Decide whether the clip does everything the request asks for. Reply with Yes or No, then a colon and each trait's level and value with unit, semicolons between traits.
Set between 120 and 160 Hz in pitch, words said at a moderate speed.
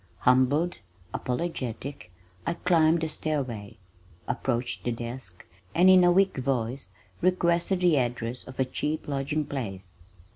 No: low, 135 Hz; slow, 130 wpm